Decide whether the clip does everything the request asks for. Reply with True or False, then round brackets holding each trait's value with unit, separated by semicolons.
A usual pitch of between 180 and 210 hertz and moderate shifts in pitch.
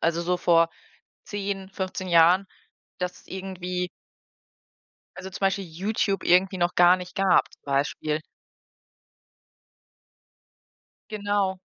False (185 Hz; 1.8 semitones)